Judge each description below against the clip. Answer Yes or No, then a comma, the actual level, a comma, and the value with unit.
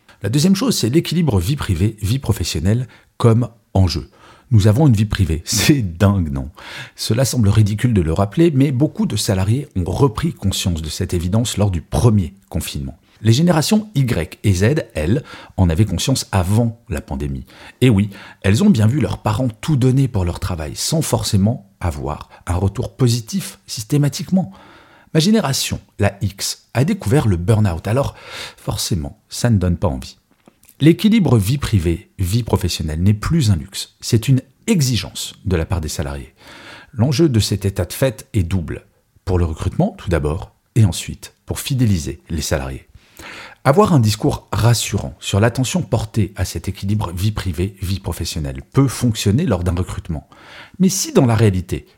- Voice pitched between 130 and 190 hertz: No, low, 105 Hz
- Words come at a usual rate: Yes, average, 165 wpm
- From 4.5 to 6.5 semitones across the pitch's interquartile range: Yes, average, 4.9 semitones